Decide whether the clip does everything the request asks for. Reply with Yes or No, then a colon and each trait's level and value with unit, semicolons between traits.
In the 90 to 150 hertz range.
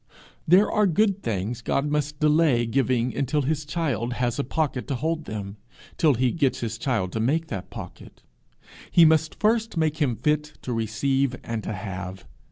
Yes: medium, 140 Hz